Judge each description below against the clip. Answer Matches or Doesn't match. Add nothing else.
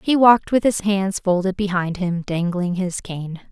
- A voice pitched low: Doesn't match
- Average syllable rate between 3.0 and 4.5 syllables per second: Matches